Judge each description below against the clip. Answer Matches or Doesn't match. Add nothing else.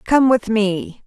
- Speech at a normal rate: Matches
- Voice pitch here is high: Matches